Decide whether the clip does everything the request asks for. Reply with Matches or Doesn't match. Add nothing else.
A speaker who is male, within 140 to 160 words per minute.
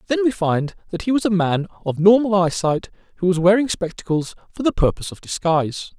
Doesn't match